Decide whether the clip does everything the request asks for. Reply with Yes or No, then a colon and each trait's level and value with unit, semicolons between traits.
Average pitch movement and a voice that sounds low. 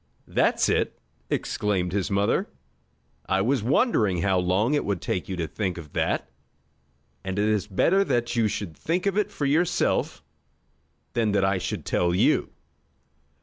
Yes: average, 4.6 semitones; low, 100 Hz